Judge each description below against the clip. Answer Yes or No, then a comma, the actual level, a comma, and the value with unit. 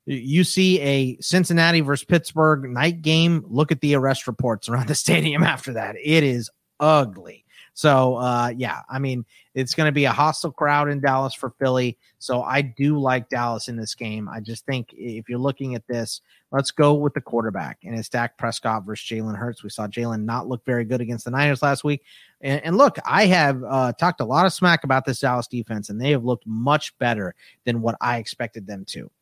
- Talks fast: Yes, fast, 215 wpm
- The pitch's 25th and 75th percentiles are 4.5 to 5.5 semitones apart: No, average, 3.8 semitones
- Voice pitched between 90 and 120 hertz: No, low, 130 Hz